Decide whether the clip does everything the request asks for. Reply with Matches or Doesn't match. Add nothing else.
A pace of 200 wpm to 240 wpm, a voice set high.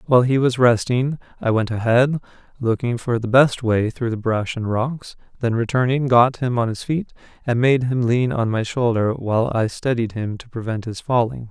Doesn't match